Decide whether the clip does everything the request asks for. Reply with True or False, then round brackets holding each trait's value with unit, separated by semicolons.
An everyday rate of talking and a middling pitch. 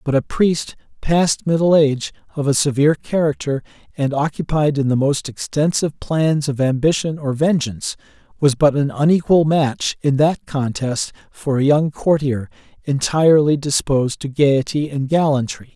True (150 wpm; 145 Hz)